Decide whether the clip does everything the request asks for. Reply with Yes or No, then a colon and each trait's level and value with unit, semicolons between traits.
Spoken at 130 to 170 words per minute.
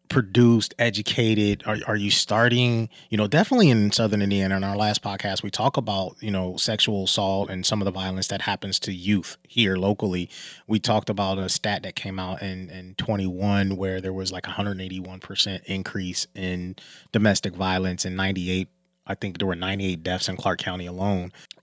No: average, 185 wpm